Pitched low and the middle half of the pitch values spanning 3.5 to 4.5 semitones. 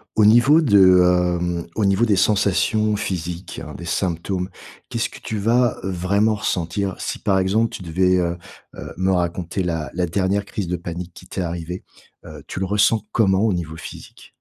No: very low, 95 Hz; average, 2.9 semitones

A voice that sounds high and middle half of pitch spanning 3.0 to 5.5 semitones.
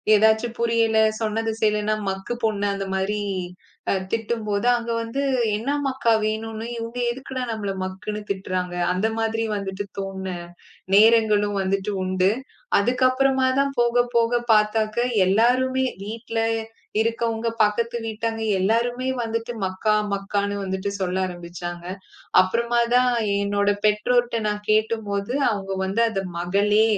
No: high, 215 Hz; narrow, 2.6 semitones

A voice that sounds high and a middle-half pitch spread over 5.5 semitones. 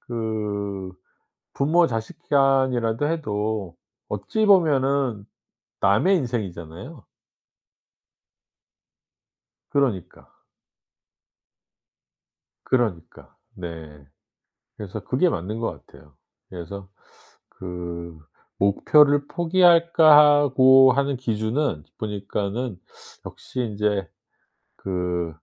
No: low, 110 Hz; wide, 6.4 semitones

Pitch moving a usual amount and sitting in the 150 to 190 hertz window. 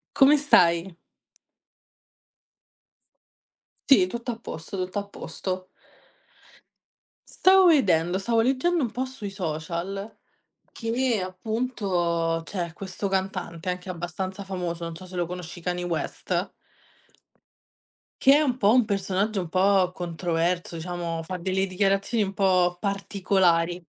Yes: average, 3.1 semitones; medium, 185 Hz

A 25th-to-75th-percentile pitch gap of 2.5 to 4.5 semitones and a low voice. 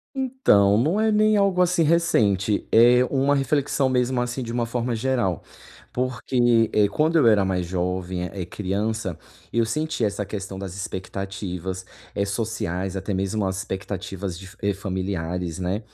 No: average, 5.0 semitones; low, 105 Hz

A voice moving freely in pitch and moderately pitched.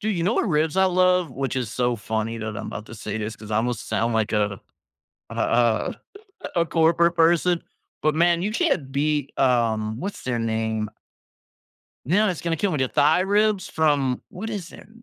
Yes: wide, 7.7 semitones; medium, 145 Hz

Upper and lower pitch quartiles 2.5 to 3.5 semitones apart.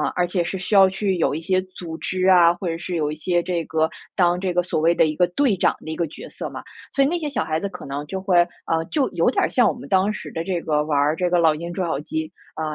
Yes: average, 2.8 semitones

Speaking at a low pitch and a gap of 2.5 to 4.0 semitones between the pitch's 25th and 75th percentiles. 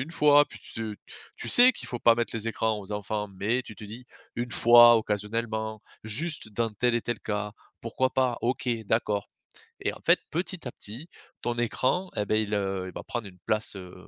Yes: low, 115 Hz; average, 2.8 semitones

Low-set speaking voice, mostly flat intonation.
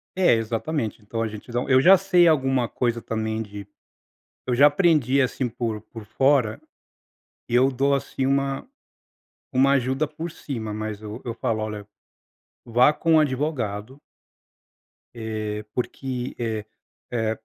No: low, 125 Hz; average, 3.9 semitones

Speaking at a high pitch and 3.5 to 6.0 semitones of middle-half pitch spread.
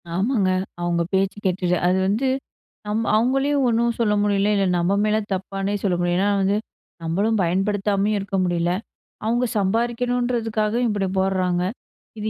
No: high, 200 Hz; average, 3.0 semitones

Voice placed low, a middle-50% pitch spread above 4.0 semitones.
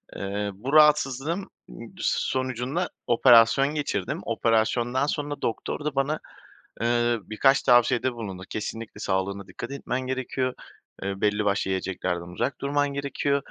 Yes: low, 120 Hz; average, 5.0 semitones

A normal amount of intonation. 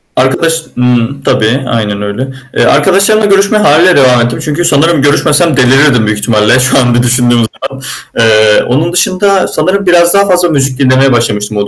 No: wide, 6.2 semitones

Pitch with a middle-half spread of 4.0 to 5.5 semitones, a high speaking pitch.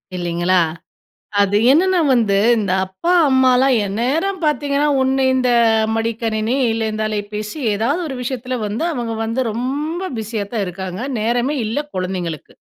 Yes: average, 4.5 semitones; high, 230 Hz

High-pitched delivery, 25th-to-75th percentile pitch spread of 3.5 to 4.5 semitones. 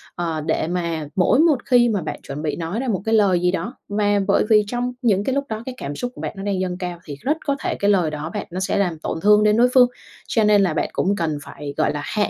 No: high, 200 Hz; average, 4.9 semitones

